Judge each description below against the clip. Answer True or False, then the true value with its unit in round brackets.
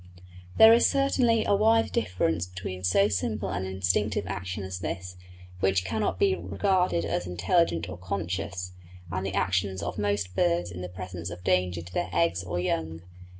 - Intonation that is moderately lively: False (2.0 semitones)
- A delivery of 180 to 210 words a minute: False (170 wpm)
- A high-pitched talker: False (90 Hz)